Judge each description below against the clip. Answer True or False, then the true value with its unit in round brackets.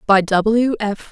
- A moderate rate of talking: True (160 wpm)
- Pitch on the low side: False (210 Hz)